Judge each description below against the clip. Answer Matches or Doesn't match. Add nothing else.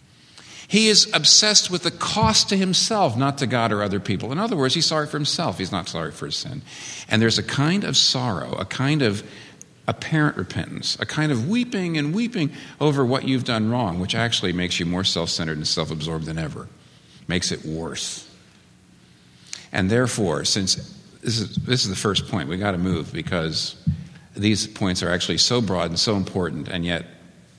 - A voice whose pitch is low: Matches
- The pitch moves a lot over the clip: Matches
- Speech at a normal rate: Matches